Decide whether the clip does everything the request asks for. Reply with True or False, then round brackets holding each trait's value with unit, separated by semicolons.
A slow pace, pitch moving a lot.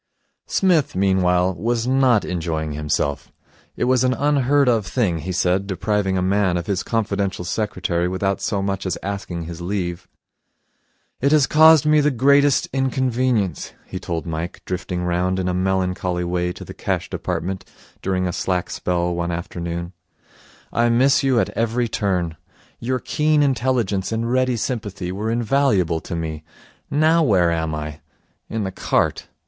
False (155 wpm; 5.8 semitones)